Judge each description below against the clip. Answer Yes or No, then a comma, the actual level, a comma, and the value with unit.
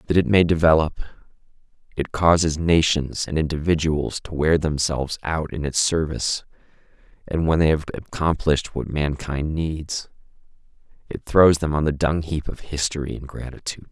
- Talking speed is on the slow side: No, average, 150 wpm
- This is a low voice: Yes, very low, 80 Hz